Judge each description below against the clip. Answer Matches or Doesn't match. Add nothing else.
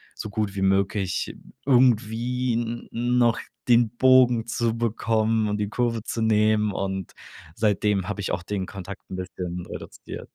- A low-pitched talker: Matches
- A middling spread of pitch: Matches